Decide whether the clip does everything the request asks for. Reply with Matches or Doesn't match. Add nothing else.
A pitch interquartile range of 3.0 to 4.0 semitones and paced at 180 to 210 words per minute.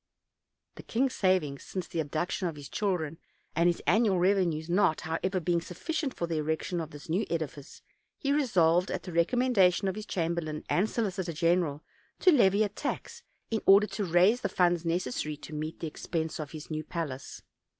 Matches